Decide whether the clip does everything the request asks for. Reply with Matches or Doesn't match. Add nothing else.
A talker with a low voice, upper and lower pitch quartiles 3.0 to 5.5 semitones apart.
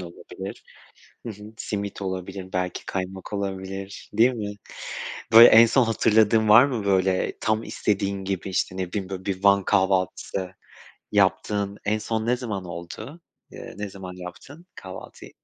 Doesn't match